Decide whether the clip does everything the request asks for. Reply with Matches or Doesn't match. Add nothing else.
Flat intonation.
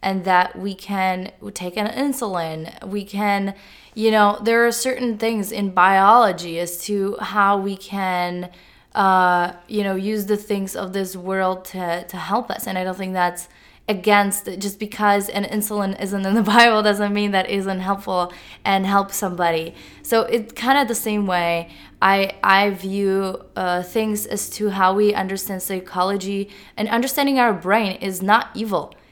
Matches